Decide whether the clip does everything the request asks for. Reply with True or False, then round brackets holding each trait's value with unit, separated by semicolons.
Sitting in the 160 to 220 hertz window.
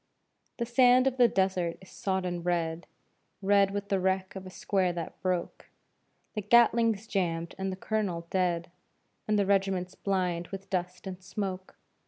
True (190 Hz)